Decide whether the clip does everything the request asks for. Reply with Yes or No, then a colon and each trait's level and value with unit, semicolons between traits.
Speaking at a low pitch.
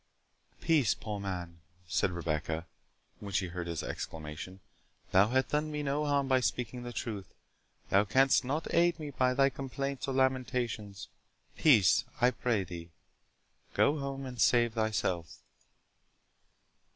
Yes: low, 120 Hz